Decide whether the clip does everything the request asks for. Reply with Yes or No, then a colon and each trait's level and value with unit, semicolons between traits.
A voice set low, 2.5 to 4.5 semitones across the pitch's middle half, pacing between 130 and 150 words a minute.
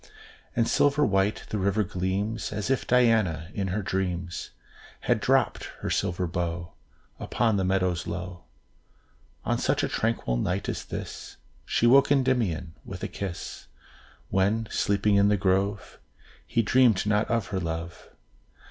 Yes: low, 100 Hz; average, 3.7 semitones; average, 145 wpm